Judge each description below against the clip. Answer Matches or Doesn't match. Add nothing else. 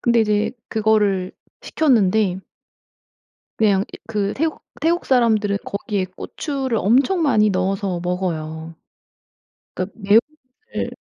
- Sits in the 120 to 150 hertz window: Doesn't match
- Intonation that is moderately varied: Matches